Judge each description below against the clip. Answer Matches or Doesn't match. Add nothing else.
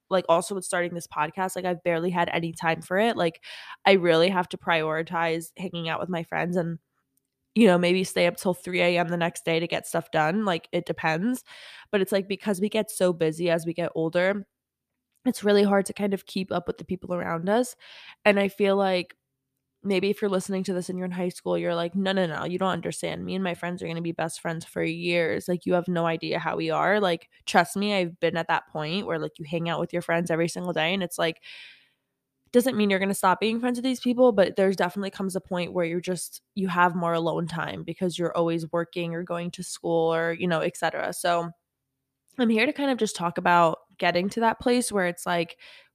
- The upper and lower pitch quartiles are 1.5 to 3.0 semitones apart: Matches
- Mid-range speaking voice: Matches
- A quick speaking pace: Matches